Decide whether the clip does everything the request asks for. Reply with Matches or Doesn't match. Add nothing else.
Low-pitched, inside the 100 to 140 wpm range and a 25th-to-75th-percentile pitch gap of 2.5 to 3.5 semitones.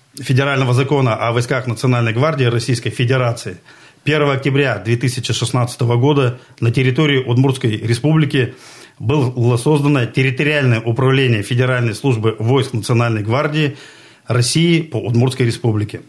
Matches